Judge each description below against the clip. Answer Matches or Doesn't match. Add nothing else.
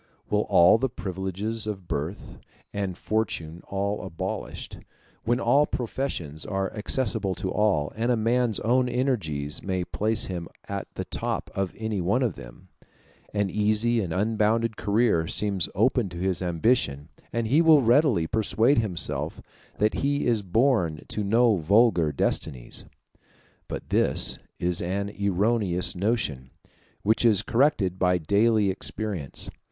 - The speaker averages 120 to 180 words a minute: Matches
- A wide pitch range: Doesn't match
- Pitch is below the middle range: Matches